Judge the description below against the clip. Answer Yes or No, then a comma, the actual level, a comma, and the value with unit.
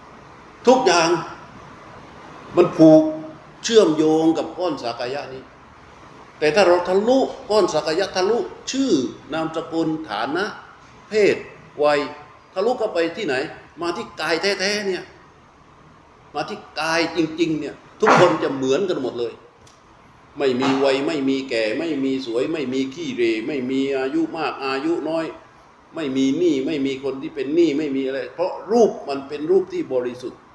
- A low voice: No, medium, 160 Hz